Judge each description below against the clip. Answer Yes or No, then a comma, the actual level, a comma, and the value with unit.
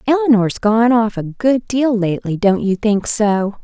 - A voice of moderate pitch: No, high, 220 Hz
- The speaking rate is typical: Yes, average, 180 wpm